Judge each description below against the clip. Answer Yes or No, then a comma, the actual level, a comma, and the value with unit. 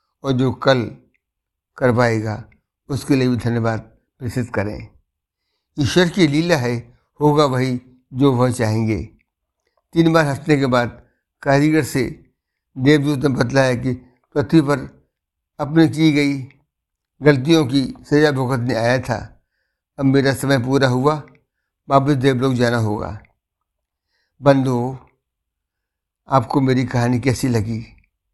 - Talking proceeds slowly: No, average, 120 wpm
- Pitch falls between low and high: No, low, 130 Hz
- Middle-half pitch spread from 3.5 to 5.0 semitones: Yes, average, 4.0 semitones